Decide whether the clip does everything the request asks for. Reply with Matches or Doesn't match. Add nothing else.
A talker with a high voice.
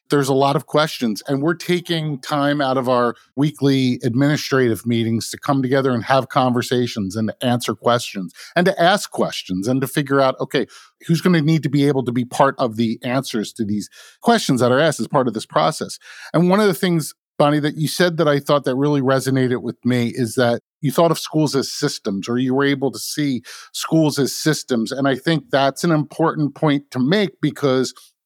Doesn't match